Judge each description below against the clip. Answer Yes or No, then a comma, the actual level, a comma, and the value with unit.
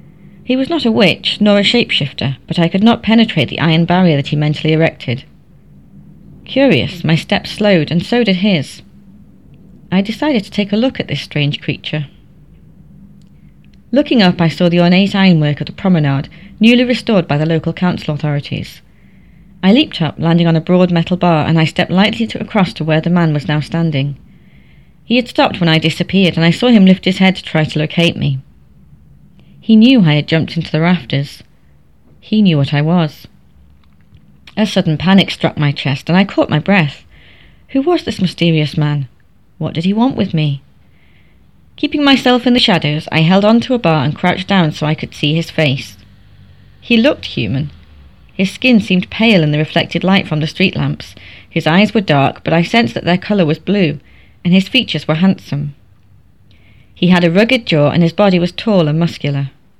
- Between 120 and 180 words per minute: No, average, 195 wpm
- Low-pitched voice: No, medium, 170 Hz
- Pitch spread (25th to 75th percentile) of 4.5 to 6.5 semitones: Yes, average, 4.9 semitones